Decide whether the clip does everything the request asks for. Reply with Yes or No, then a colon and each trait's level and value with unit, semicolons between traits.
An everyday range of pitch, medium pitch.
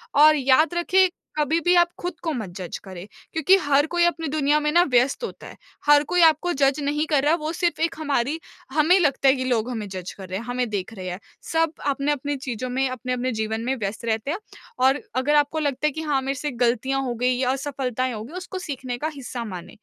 No: average, 3.9 semitones; very high, 275 Hz